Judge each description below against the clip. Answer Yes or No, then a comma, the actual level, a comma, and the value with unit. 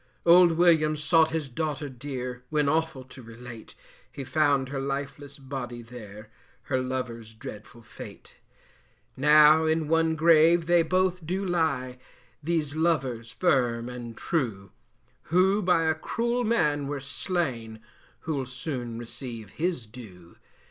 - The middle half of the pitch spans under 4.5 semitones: No, average, 4.8 semitones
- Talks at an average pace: No, slow, 130 wpm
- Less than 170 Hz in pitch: Yes, medium, 140 Hz